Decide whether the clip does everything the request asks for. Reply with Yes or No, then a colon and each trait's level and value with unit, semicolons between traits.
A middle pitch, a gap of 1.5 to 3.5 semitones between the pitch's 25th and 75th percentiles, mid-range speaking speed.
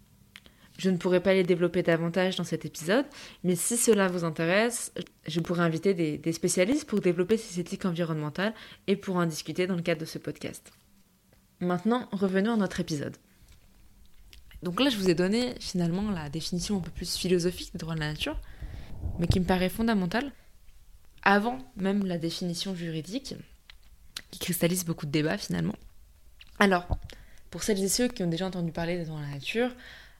Yes: medium, 180 Hz; average, 3.1 semitones; average, 180 wpm